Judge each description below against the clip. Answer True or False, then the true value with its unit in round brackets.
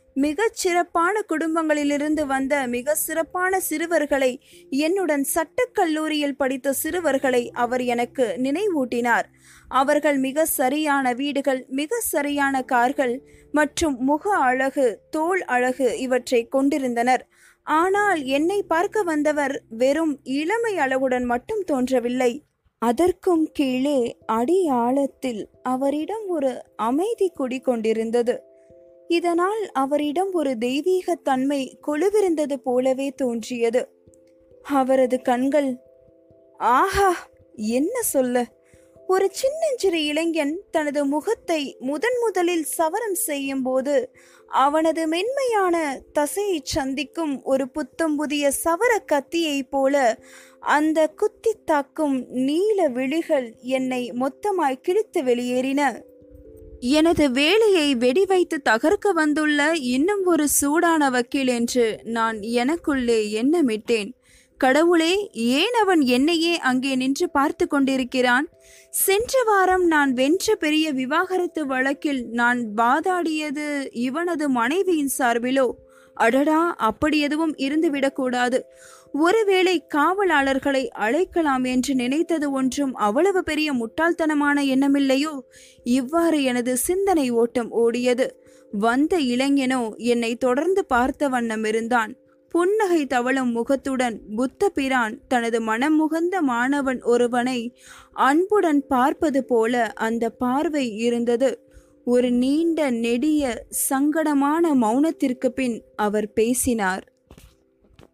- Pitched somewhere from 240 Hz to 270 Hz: False (280 Hz)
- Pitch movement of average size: True (4.5 semitones)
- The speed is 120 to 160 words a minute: False (95 wpm)